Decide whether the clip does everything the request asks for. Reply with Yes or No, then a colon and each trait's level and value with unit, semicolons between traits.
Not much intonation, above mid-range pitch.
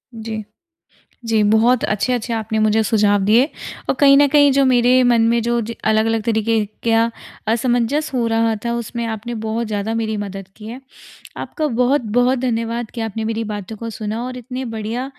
Yes: narrow, 2.1 semitones; high, 230 Hz